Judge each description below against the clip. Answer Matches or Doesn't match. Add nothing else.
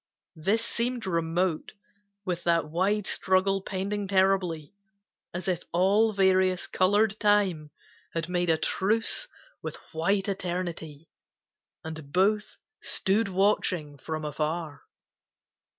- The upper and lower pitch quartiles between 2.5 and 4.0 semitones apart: Matches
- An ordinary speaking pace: Doesn't match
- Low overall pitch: Doesn't match